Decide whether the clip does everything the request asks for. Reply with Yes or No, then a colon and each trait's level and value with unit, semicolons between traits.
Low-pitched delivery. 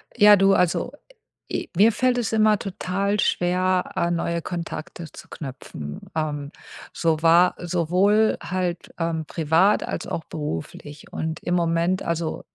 No: medium, 175 Hz